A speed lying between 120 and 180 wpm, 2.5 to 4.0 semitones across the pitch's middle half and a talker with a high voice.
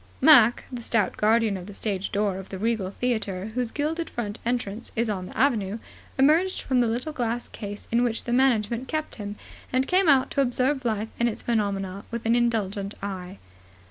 No: average, 195 wpm; average, 3.6 semitones; high, 230 Hz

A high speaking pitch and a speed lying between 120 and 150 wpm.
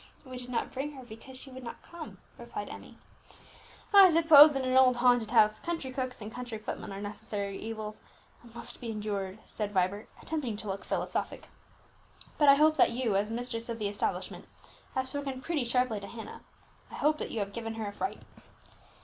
No: high, 240 Hz; average, 200 wpm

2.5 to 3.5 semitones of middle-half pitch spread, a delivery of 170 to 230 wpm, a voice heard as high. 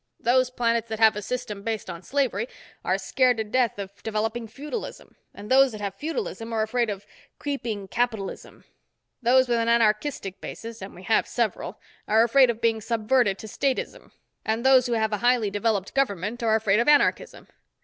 Yes: average, 2.8 semitones; average, 175 wpm; high, 230 Hz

